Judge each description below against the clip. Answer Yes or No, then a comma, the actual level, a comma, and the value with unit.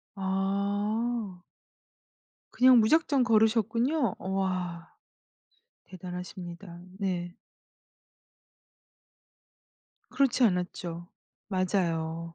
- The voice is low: No, high, 195 Hz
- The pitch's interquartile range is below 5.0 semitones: Yes, average, 4.2 semitones